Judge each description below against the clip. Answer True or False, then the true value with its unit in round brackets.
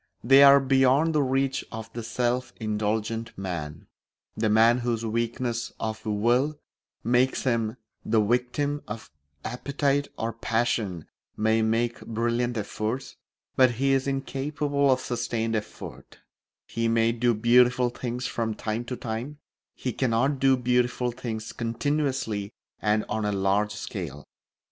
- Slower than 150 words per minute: True (135 wpm)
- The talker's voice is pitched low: True (120 Hz)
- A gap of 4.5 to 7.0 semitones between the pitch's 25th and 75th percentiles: False (2.7 semitones)